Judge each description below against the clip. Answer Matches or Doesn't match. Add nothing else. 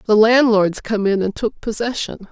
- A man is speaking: Doesn't match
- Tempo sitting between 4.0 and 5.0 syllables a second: Matches